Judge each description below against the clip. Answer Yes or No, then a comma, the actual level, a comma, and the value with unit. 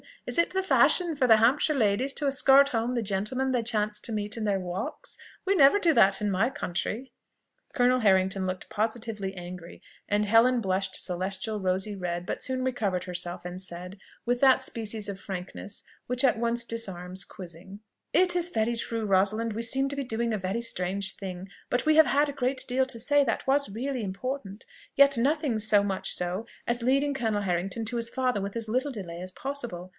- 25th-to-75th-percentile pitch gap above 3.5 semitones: Yes, average, 5.1 semitones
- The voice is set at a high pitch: Yes, high, 225 Hz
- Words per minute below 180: No, average, 200 wpm